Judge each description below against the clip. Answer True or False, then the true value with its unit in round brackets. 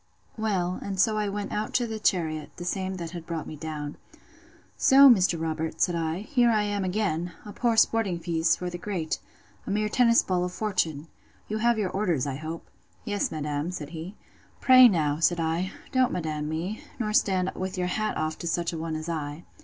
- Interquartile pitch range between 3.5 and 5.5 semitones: True (4.6 semitones)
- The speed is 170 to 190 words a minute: False (200 wpm)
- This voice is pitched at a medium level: True (180 Hz)